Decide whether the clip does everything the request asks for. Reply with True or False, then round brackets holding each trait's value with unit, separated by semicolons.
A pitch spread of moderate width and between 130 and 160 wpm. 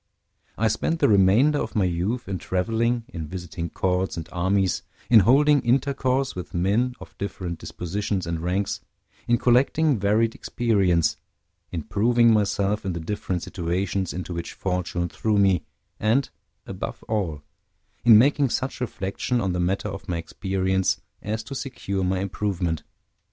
True (4.5 semitones; 150 wpm)